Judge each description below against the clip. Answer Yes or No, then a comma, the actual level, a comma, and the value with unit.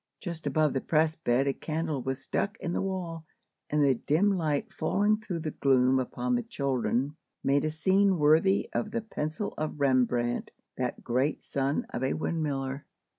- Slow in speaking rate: No, average, 175 wpm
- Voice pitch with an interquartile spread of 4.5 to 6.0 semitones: Yes, average, 4.9 semitones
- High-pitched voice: No, medium, 155 Hz